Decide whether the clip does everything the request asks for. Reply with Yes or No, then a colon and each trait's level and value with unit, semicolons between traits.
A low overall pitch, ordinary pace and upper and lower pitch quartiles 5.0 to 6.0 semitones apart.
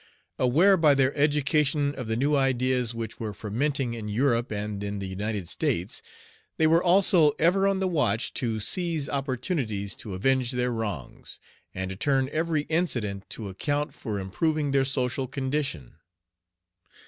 Yes: low, 130 Hz; average, 155 wpm; wide, 5.6 semitones